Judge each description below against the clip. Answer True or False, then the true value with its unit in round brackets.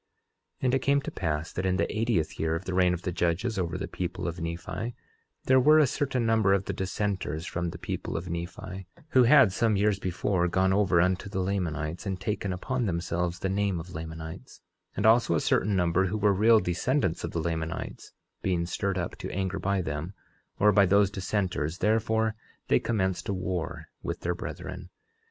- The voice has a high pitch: False (95 Hz)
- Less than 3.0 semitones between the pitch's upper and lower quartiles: False (3.3 semitones)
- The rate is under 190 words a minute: False (200 wpm)